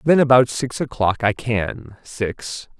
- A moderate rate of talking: Yes, average, 150 wpm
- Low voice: Yes, low, 120 Hz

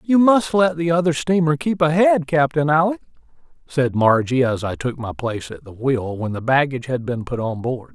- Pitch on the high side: No, medium, 145 Hz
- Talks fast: Yes, fast, 210 wpm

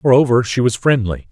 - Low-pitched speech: Yes, low, 120 Hz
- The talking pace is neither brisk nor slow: Yes, average, 185 wpm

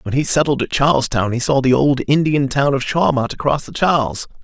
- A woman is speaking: No, male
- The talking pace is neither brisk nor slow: No, fast, 215 wpm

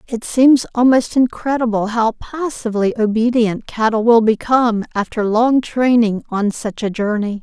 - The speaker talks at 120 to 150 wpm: Yes, slow, 135 wpm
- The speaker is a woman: Yes, female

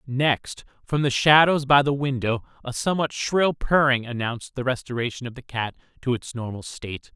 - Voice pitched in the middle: No, low, 130 Hz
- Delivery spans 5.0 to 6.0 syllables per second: Yes, 5.2 syllables/s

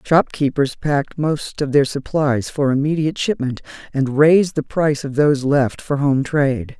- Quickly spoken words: No, average, 170 wpm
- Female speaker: Yes, female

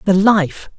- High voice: Yes, high, 195 Hz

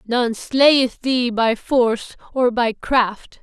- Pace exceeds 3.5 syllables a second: No, 3.0 syllables/s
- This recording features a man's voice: No, female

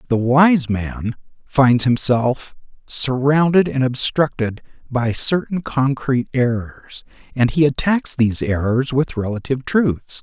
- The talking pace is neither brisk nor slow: No, slow, 115 wpm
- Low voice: Yes, low, 130 Hz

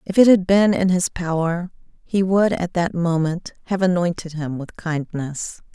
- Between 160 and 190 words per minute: Yes, average, 175 wpm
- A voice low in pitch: No, medium, 175 Hz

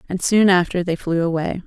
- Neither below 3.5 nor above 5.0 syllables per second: No, 5.4 syllables/s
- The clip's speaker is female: Yes, female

